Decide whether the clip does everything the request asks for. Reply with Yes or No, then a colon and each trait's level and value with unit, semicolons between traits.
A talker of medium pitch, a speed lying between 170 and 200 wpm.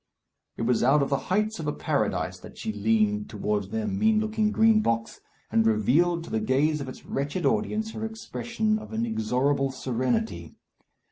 Yes: medium, 145 Hz; average, 175 wpm